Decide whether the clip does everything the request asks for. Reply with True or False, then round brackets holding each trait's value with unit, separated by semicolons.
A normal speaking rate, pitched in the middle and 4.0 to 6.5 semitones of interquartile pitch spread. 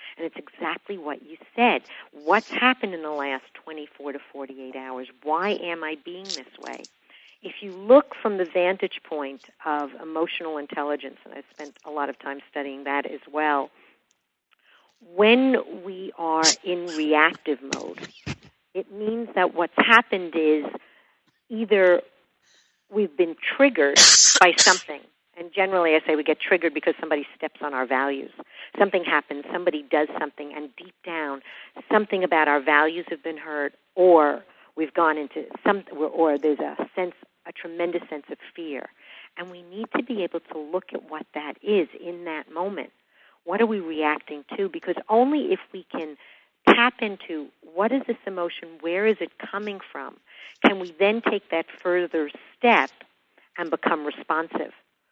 True (160 wpm; 170 Hz; 4.4 semitones)